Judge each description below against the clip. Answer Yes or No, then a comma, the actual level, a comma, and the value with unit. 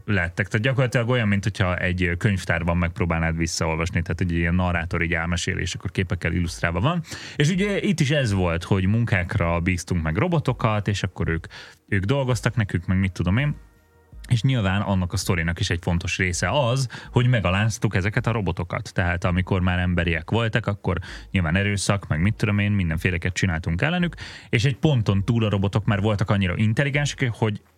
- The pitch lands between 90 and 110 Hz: Yes, low, 100 Hz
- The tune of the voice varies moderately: Yes, average, 4.7 semitones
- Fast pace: Yes, fast, 175 wpm